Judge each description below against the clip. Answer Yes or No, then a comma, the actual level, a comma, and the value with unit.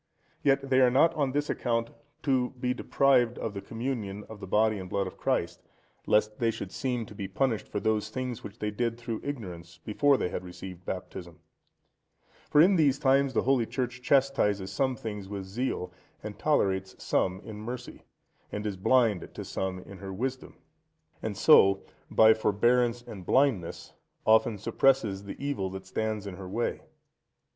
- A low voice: Yes, low, 110 Hz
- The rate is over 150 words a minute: Yes, average, 175 wpm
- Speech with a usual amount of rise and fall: Yes, average, 4.6 semitones